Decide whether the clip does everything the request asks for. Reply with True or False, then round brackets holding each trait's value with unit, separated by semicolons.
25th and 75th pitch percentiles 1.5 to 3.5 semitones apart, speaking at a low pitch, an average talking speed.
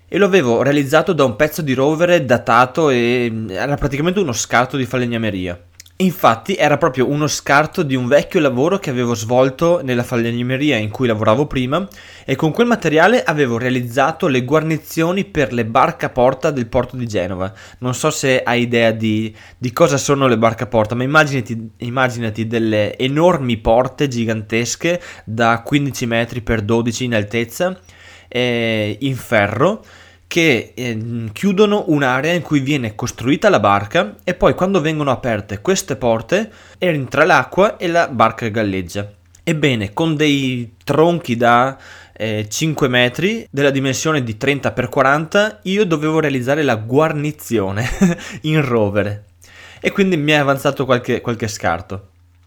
False (5.2 semitones; 130 Hz; 150 wpm)